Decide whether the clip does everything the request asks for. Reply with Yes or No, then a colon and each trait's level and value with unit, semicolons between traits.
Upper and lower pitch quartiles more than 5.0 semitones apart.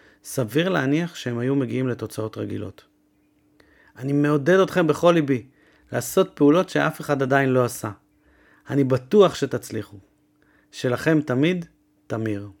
Yes: wide, 5.5 semitones